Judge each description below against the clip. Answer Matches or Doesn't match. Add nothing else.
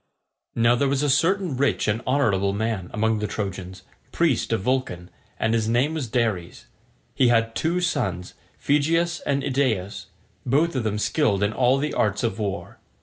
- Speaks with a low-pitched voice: Matches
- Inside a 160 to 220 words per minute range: Matches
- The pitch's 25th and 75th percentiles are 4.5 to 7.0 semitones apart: Matches